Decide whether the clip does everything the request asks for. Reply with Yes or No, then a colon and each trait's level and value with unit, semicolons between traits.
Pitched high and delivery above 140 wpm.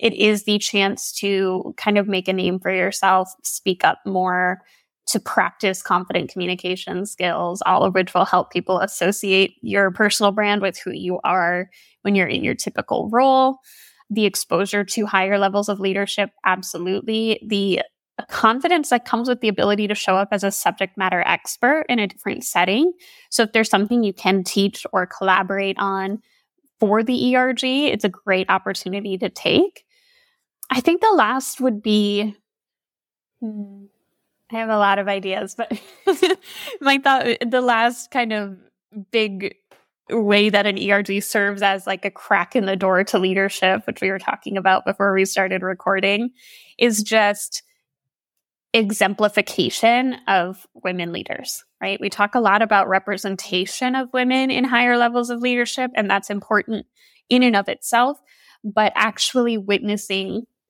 Yes: high, 205 Hz; average, 155 wpm